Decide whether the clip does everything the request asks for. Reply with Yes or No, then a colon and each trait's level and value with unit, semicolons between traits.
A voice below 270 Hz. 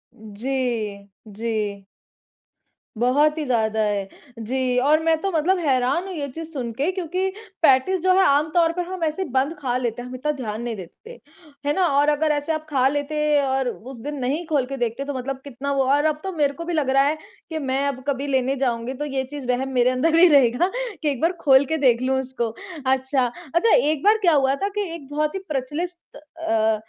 No: very high, 275 Hz